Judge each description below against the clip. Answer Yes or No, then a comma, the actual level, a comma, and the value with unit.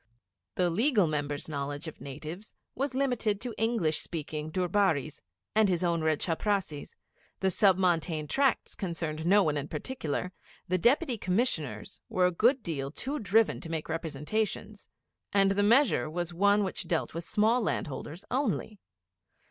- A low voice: No, medium, 180 Hz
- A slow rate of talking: No, average, 155 wpm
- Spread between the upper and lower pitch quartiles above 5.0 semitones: Yes, wide, 5.4 semitones